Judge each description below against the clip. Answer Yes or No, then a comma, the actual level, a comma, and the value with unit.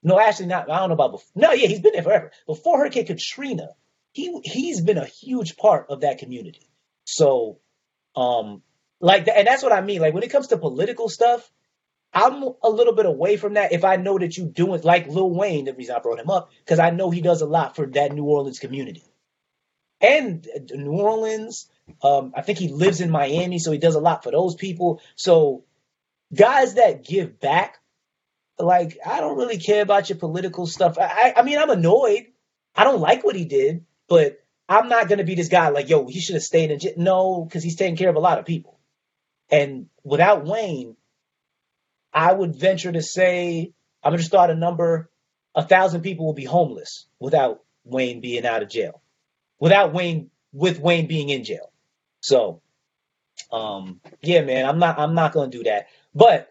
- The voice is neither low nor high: Yes, medium, 180 Hz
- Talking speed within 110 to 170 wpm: No, fast, 205 wpm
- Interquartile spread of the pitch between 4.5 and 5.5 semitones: Yes, average, 4.9 semitones